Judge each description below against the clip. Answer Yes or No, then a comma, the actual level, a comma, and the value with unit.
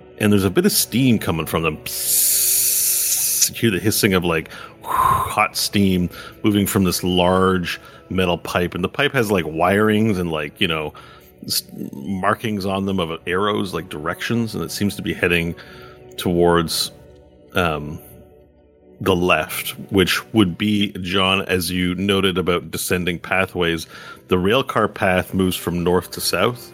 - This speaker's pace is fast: No, average, 155 wpm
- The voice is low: Yes, very low, 90 Hz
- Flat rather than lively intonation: No, average, 3.7 semitones